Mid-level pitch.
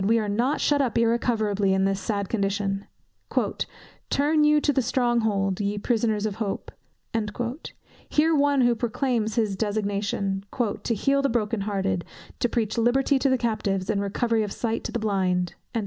No: high, 220 Hz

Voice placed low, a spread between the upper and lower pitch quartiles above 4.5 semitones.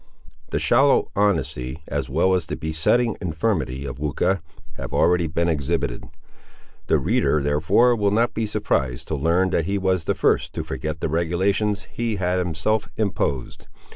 Yes: very low, 90 Hz; average, 4.9 semitones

